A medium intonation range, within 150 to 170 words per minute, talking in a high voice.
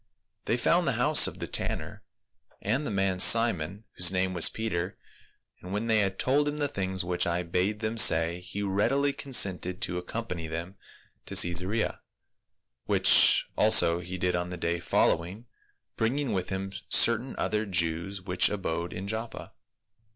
No: average, 4.1 semitones; average, 160 wpm; very low, 95 Hz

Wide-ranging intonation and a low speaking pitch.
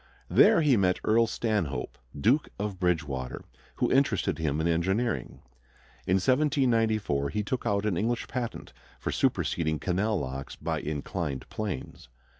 Yes: wide, 6.5 semitones; low, 100 Hz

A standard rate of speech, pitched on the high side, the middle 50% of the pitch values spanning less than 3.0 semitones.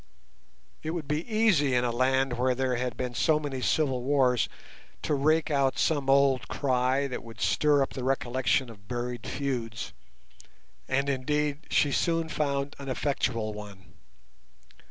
No: average, 155 wpm; low, 135 Hz; narrow, 2.6 semitones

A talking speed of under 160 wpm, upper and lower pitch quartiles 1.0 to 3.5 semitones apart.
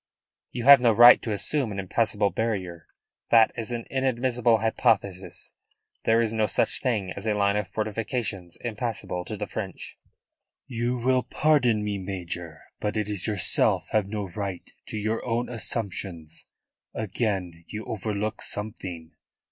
Yes: average, 150 wpm; average, 3.1 semitones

